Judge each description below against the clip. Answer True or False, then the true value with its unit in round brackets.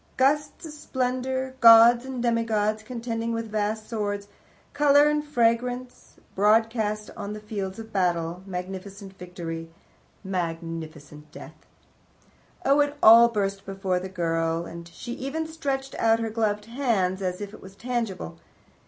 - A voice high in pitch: True (215 Hz)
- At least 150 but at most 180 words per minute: False (135 wpm)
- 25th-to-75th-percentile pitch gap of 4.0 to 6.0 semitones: True (4.6 semitones)